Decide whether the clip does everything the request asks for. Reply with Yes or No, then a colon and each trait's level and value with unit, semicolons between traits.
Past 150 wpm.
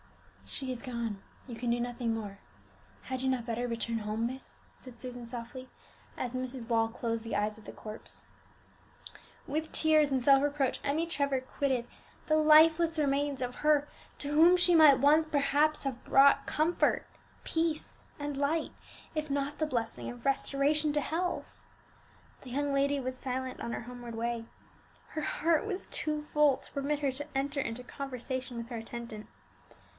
Yes: average, 170 wpm